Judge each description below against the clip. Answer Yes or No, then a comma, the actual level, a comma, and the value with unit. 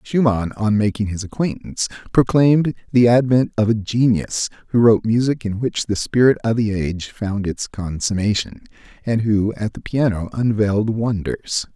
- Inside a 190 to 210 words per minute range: No, average, 160 wpm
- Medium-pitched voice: No, low, 110 Hz